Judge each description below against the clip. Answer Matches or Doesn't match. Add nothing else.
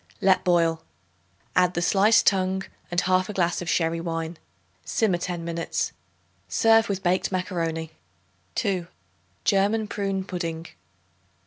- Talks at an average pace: Doesn't match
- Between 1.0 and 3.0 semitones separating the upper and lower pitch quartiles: Matches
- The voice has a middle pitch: Matches